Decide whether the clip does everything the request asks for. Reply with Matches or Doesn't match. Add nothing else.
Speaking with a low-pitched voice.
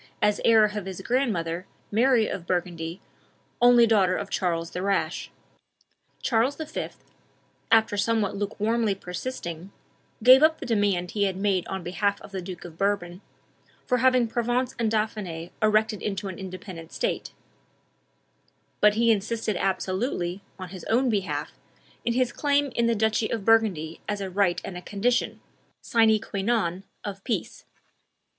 Doesn't match